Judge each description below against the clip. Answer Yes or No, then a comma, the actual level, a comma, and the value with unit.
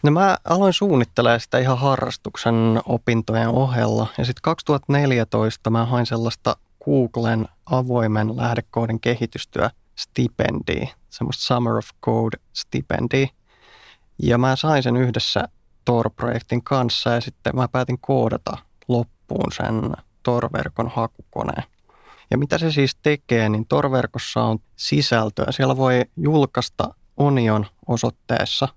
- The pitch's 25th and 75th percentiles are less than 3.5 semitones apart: Yes, narrow, 2.6 semitones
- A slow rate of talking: No, average, 115 wpm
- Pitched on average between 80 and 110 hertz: No, low, 120 Hz